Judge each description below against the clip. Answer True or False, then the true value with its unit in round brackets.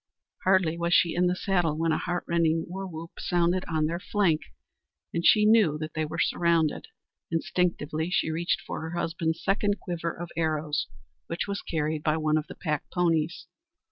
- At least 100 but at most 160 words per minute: False (175 wpm)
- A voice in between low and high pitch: True (165 Hz)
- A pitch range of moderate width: False (2.1 semitones)